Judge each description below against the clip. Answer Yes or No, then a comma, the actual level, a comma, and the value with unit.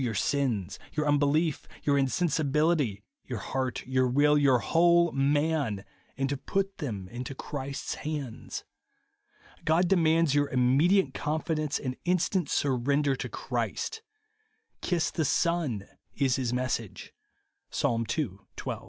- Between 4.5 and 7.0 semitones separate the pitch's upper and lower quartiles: No, average, 3.9 semitones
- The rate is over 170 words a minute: No, slow, 135 wpm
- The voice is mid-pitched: Yes, medium, 145 Hz